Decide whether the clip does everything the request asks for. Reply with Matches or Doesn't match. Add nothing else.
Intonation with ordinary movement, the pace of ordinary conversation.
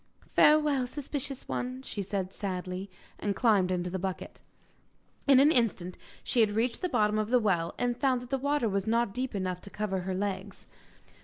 Matches